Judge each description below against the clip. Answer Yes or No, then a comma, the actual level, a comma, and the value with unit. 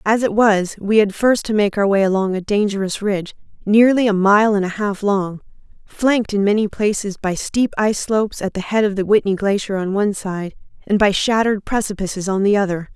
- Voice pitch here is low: No, high, 205 Hz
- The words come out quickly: Yes, fast, 215 wpm